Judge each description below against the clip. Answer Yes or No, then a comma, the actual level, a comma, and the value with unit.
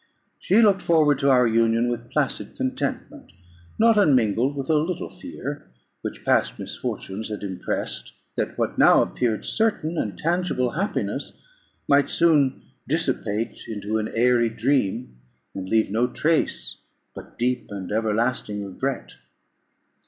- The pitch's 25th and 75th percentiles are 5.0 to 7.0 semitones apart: Yes, wide, 5.6 semitones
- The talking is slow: Yes, slow, 130 wpm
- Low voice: Yes, low, 125 Hz